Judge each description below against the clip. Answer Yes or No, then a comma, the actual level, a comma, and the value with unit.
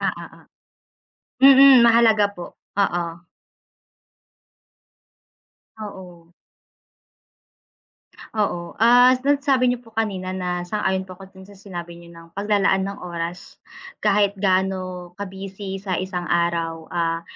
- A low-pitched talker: No, high, 190 Hz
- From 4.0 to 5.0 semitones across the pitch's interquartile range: No, average, 3.1 semitones